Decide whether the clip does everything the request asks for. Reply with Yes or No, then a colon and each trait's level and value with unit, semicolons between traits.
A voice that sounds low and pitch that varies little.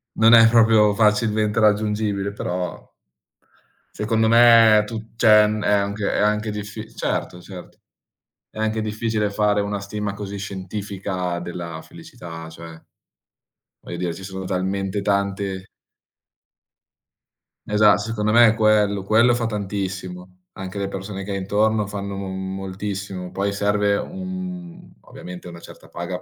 Yes: low, 100 Hz; narrow, 2.1 semitones